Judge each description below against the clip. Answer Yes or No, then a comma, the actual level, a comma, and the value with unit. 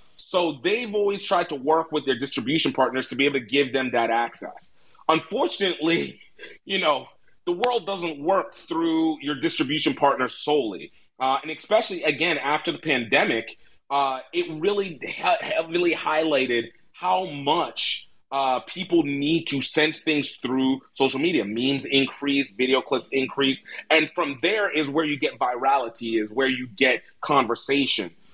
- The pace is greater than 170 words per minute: No, average, 150 wpm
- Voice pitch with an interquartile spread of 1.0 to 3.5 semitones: No, average, 3.9 semitones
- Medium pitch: Yes, medium, 150 Hz